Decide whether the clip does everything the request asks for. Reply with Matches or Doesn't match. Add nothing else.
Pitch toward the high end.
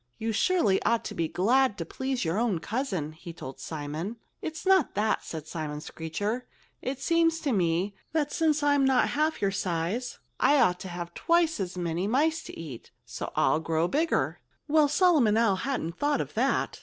Matches